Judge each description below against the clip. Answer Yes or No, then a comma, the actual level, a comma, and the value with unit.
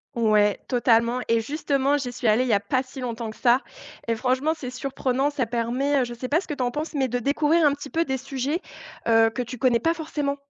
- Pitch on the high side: Yes, very high, 255 Hz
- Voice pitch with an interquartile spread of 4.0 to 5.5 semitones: No, average, 3.3 semitones